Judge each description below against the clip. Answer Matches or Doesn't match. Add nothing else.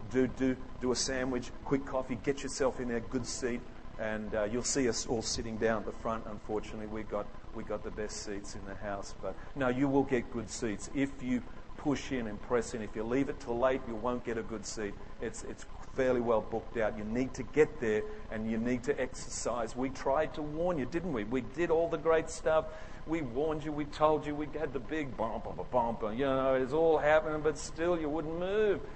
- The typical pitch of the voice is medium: Doesn't match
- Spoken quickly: Matches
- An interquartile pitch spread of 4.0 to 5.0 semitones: Matches